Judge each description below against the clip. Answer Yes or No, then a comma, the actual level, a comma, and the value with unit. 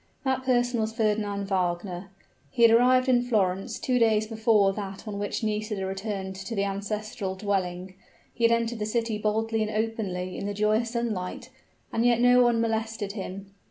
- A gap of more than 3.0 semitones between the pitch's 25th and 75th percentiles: No, average, 2.7 semitones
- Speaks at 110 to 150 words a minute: No, average, 180 wpm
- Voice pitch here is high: Yes, high, 215 Hz